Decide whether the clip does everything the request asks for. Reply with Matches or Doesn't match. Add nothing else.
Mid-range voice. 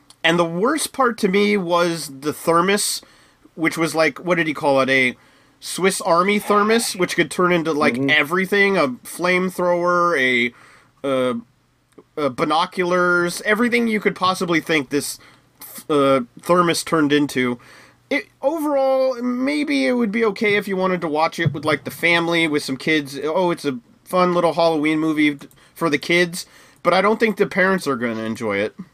Matches